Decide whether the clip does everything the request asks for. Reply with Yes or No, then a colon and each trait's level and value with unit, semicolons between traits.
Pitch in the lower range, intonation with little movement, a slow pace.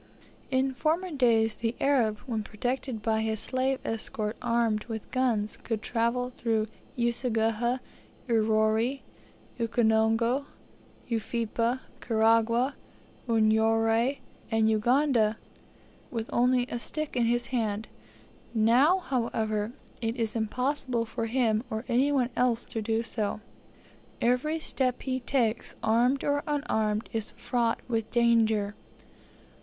No: high, 230 Hz; narrow, 2.3 semitones; slow, 115 wpm